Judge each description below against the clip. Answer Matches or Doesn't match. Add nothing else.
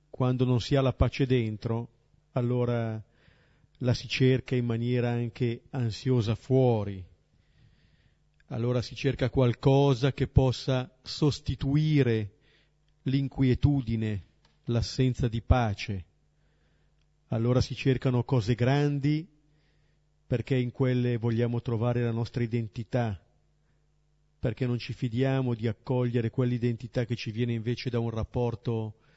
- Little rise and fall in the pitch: Matches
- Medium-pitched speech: Doesn't match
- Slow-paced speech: Matches